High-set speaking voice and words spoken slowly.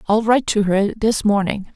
No: high, 210 Hz; fast, 205 wpm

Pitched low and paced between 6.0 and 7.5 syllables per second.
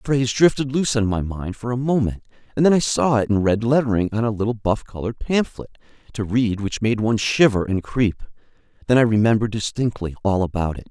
Yes: low, 110 Hz; 6.1 syllables/s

